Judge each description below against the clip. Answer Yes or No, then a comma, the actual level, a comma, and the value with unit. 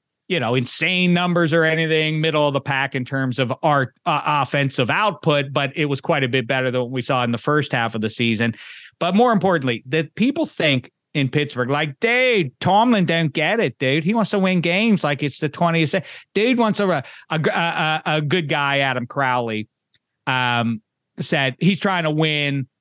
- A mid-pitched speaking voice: Yes, medium, 150 Hz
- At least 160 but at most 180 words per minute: No, average, 195 wpm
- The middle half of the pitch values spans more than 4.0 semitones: Yes, average, 4.6 semitones